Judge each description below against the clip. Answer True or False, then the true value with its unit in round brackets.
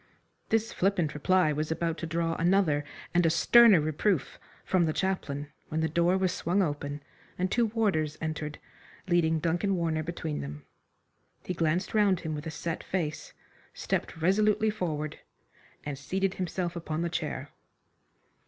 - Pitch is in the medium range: True (170 Hz)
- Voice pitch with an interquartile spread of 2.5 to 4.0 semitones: True (3.3 semitones)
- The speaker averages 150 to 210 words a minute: True (155 wpm)